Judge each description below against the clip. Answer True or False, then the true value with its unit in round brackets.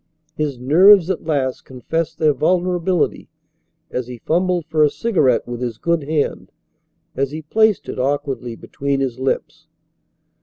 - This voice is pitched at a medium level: True (150 Hz)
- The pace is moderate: True (145 wpm)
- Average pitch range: True (4.6 semitones)